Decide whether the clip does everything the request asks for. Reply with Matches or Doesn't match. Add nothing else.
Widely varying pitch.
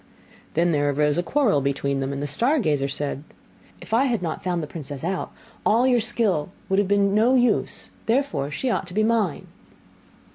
Matches